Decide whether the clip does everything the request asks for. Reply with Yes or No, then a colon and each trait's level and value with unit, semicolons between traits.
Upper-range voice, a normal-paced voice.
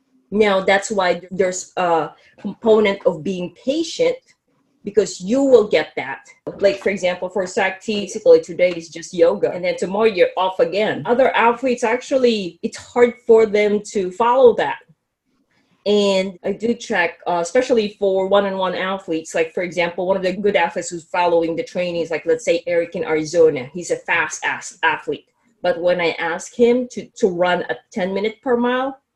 Yes: high, 205 Hz; average, 180 wpm